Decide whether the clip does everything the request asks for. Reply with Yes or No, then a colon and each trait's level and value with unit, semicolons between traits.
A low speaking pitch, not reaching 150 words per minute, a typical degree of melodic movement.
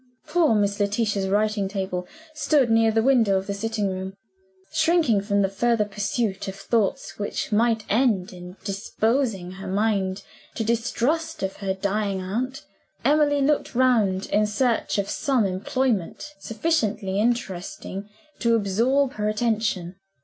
No: high, 210 Hz; average, 140 wpm; average, 3.6 semitones